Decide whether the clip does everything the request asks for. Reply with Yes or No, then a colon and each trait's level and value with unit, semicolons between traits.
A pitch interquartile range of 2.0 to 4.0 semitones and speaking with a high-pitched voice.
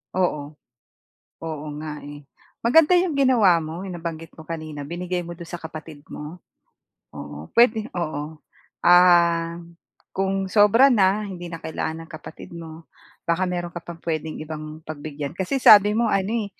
No: average, 3.5 semitones; medium, 170 Hz